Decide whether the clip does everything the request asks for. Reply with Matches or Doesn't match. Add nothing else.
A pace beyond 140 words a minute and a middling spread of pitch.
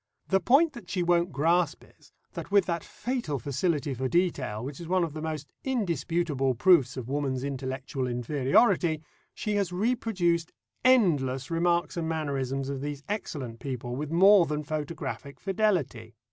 Matches